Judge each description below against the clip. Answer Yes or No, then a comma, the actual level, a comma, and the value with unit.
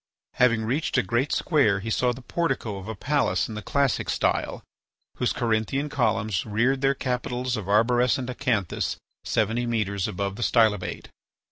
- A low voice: Yes, low, 120 Hz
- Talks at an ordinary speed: Yes, average, 155 wpm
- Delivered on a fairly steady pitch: No, average, 3.1 semitones